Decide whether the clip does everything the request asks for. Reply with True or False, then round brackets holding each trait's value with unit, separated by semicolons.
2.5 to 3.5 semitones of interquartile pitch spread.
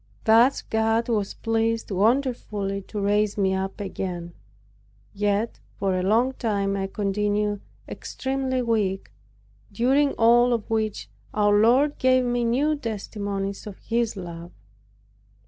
True (3.2 semitones)